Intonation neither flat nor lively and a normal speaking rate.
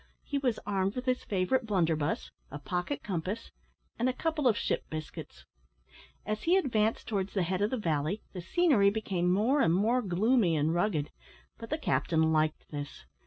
No: wide, 6.3 semitones; average, 175 wpm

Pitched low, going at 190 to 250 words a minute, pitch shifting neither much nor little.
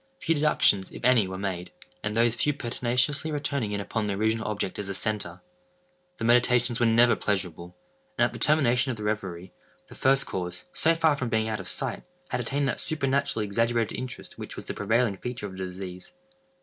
Yes: low, 115 Hz; average, 200 wpm; average, 4.4 semitones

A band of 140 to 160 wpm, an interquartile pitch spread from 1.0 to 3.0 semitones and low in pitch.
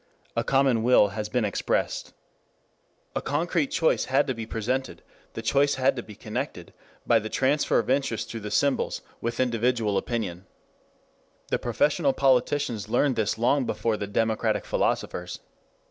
No: average, 150 wpm; average, 3.6 semitones; low, 120 Hz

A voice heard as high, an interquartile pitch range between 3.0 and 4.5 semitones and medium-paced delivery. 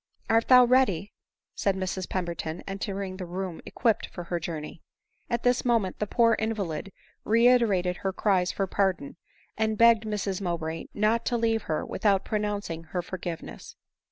Yes: high, 195 Hz; average, 3.8 semitones; average, 165 wpm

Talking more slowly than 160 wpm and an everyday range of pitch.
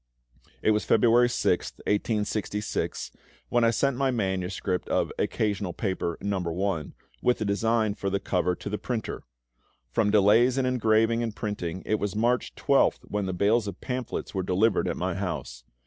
No: average, 165 wpm; average, 3.0 semitones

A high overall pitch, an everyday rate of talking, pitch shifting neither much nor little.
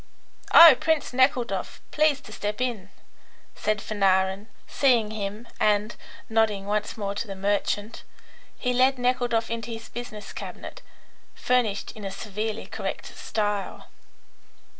No: high, 215 Hz; slow, 125 wpm; average, 3.1 semitones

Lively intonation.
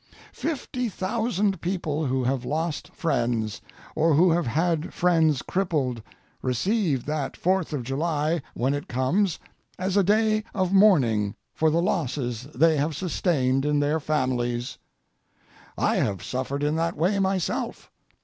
Yes: wide, 5.7 semitones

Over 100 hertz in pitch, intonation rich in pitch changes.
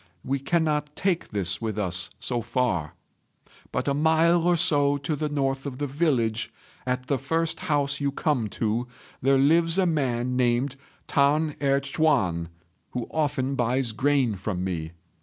No: low, 135 Hz; average, 4.0 semitones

